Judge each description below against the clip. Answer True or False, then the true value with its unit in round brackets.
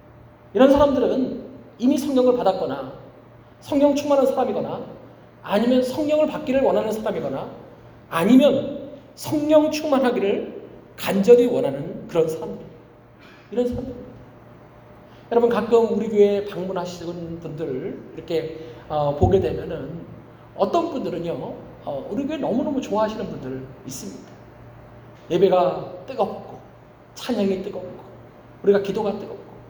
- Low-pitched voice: False (220 Hz)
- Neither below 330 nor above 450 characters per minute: False (285 characters per minute)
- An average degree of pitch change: False (6.9 semitones)